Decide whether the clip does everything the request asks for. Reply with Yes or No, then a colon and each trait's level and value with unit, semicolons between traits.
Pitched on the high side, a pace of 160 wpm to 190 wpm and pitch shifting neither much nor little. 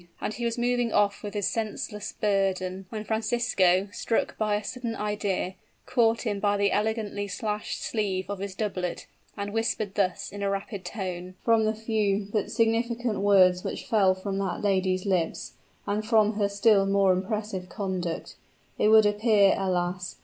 No: high, 205 Hz; average, 165 wpm; narrow, 2.3 semitones